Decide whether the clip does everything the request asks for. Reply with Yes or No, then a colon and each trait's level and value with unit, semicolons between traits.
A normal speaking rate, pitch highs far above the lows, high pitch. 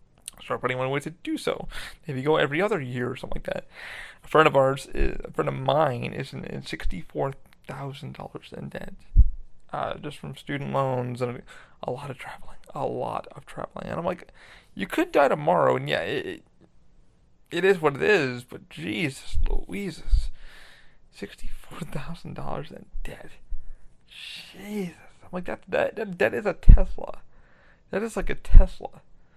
No: average, 170 wpm; wide, 6.2 semitones; medium, 150 Hz